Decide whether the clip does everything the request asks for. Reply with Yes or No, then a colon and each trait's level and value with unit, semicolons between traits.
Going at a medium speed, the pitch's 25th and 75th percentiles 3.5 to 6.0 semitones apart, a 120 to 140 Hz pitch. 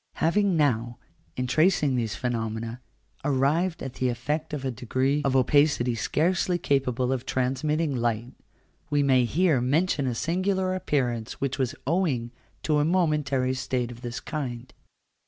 Yes: average, 145 wpm; average, 4.0 semitones; low, 135 Hz